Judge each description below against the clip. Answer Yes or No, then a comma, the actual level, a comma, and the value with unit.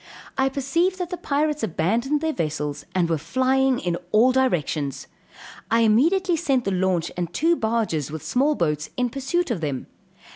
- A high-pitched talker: Yes, high, 235 Hz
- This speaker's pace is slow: No, average, 170 wpm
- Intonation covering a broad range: Yes, wide, 9.0 semitones